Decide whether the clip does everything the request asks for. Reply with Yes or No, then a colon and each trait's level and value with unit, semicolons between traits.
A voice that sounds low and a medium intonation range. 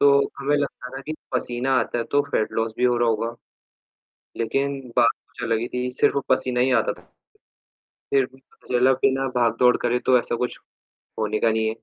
No: low, 125 Hz; narrow, 2.3 semitones